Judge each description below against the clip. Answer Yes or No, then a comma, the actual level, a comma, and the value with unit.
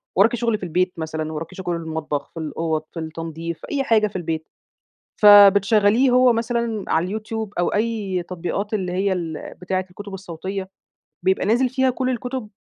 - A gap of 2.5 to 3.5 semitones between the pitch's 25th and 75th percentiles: No, average, 4.9 semitones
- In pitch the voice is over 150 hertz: Yes, high, 190 Hz